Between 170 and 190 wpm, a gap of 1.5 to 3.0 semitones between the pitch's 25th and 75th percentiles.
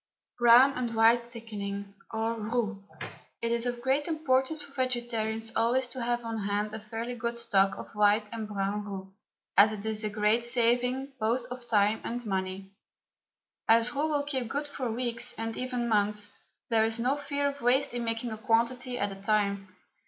Yes: average, 180 wpm; average, 2.7 semitones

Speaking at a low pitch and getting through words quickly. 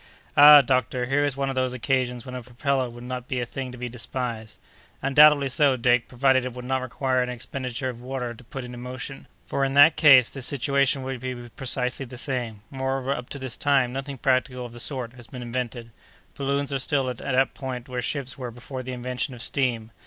Yes: low, 130 Hz; fast, 220 wpm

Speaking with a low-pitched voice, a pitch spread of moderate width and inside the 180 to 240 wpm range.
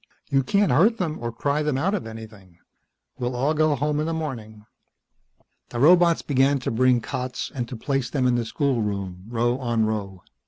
Yes: low, 125 Hz; average, 4.9 semitones; average, 190 wpm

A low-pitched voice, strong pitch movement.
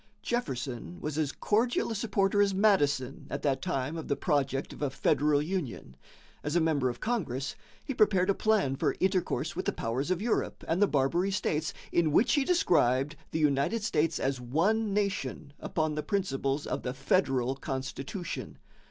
No: medium, 155 Hz; wide, 6.4 semitones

